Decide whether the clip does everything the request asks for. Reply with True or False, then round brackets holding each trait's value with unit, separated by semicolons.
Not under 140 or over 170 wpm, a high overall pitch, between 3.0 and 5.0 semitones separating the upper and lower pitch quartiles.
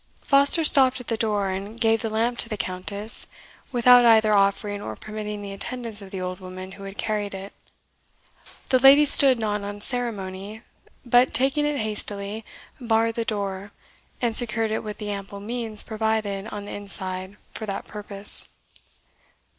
False (165 wpm; 215 Hz; 2.6 semitones)